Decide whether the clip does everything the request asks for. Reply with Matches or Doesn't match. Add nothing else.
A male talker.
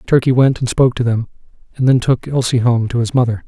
Matches